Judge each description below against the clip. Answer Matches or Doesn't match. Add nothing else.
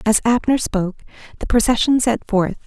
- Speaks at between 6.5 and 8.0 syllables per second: Doesn't match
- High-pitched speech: Matches